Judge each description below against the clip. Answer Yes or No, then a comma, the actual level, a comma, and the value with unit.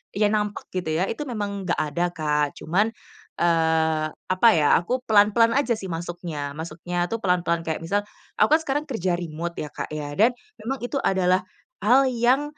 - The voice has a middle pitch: Yes, medium, 180 Hz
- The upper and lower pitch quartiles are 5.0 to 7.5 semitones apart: Yes, wide, 5.5 semitones